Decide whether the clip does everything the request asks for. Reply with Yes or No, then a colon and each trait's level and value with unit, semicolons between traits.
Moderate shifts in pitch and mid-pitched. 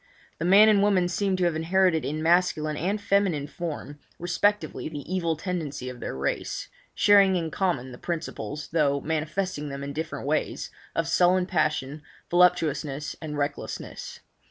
Yes: average, 3.7 semitones; medium, 160 Hz